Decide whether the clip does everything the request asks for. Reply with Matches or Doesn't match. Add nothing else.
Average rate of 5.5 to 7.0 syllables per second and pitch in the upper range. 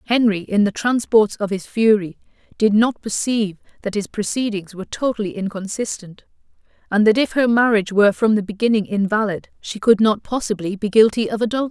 Matches